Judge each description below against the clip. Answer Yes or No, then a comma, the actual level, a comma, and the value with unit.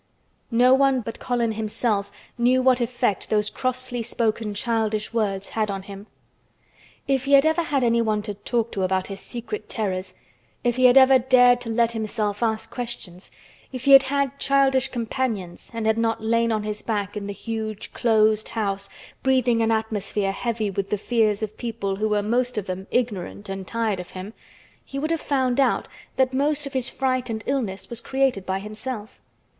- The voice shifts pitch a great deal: No, average, 3.4 semitones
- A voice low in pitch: No, high, 230 Hz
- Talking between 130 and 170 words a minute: No, average, 180 wpm